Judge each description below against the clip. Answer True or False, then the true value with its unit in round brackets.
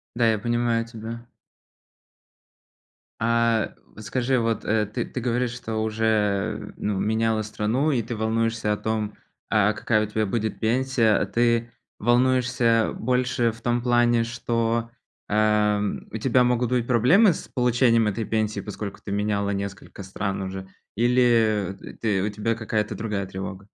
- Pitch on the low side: True (115 Hz)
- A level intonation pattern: True (2.1 semitones)